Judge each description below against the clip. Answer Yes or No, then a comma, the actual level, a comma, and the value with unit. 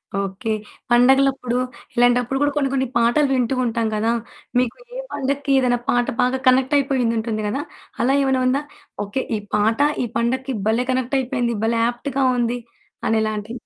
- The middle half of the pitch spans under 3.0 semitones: Yes, narrow, 2.5 semitones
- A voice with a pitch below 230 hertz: No, high, 245 Hz